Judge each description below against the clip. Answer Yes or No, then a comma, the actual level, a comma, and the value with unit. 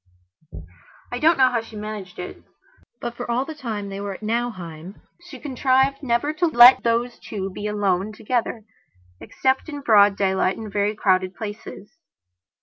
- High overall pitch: Yes, high, 220 Hz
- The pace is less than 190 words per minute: Yes, average, 160 wpm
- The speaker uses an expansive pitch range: No, average, 4.1 semitones